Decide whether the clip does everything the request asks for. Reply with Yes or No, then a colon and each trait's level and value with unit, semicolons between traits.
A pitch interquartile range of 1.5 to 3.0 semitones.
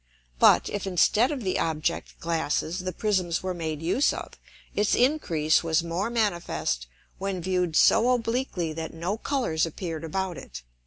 No: average, 4.3 semitones